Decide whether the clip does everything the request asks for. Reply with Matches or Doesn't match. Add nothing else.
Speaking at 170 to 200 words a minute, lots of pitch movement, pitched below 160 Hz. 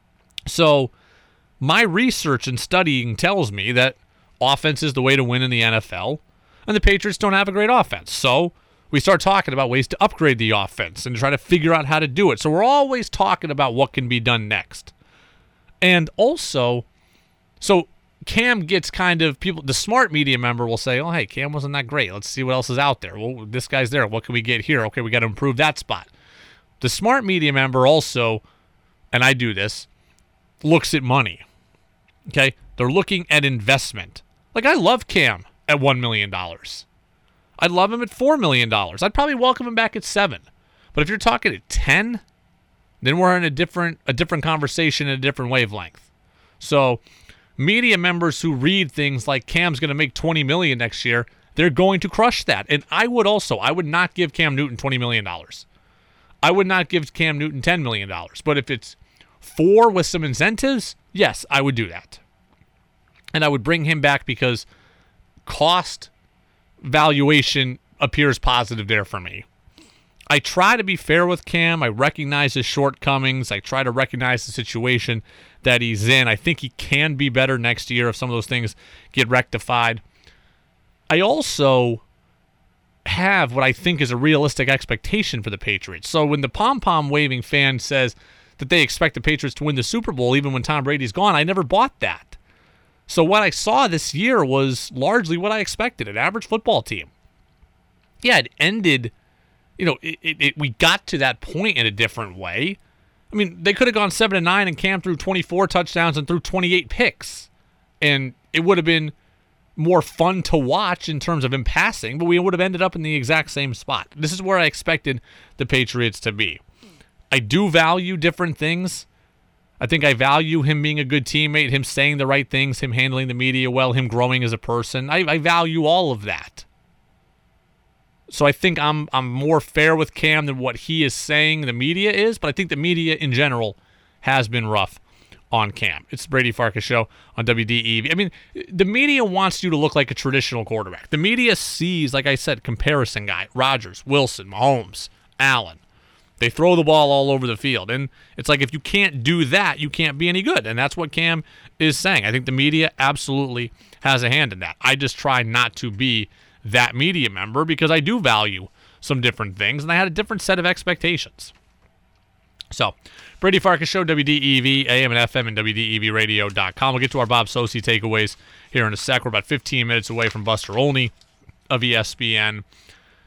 Matches